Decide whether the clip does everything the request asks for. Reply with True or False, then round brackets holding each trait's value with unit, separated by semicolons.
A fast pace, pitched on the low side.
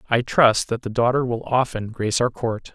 True (220 wpm; 120 Hz)